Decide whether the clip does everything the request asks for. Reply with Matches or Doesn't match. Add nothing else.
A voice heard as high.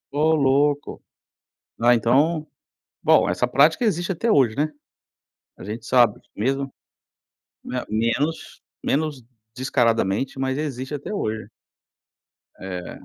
Doesn't match